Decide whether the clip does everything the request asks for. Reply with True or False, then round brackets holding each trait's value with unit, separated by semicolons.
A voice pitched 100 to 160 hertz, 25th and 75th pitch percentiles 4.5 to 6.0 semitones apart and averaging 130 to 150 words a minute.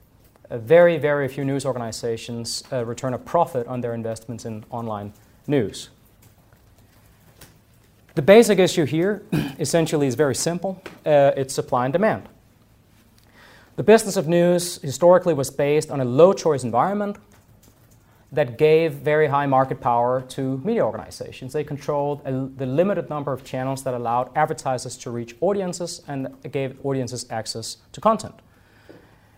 True (135 Hz; 4.9 semitones; 145 wpm)